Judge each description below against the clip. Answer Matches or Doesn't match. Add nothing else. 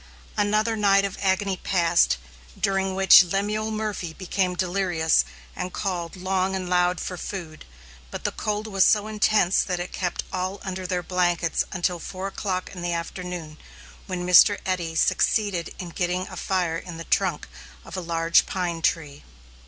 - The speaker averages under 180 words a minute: Matches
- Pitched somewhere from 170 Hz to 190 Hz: Matches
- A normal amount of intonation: Doesn't match